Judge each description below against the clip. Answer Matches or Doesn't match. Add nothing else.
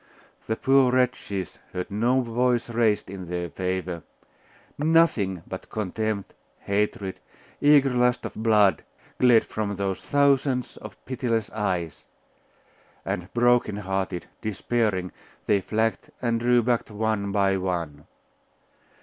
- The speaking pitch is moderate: Doesn't match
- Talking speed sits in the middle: Doesn't match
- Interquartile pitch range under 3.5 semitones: Doesn't match